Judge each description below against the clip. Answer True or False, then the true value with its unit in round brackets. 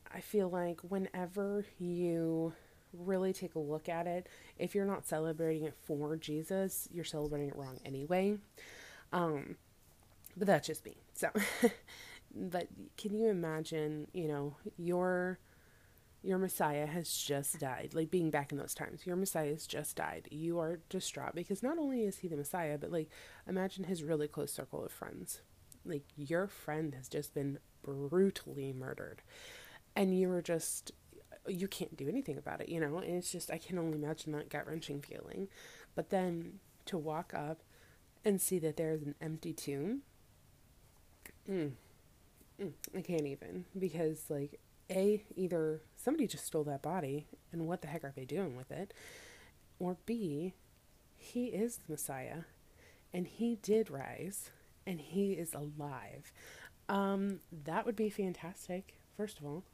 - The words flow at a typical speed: True (160 wpm)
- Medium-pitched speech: True (170 Hz)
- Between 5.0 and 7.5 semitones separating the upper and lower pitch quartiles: False (4.1 semitones)